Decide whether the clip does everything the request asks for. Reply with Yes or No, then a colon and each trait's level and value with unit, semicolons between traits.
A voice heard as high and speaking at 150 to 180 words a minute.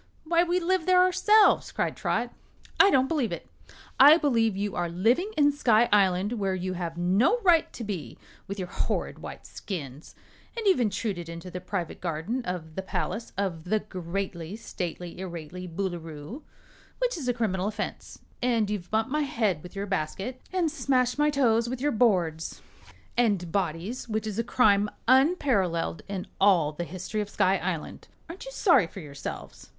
Yes: high, 205 Hz; average, 175 wpm